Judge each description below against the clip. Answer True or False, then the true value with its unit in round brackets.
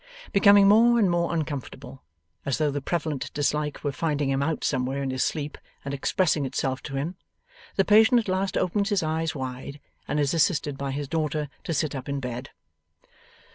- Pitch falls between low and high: True (150 Hz)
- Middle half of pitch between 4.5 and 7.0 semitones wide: False (4.0 semitones)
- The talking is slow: False (185 wpm)